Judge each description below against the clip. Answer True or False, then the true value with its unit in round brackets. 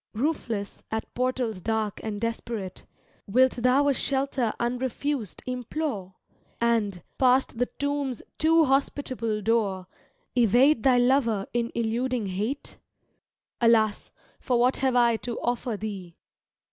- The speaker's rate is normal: False (115 wpm)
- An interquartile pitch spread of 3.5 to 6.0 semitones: False (3.1 semitones)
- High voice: True (235 Hz)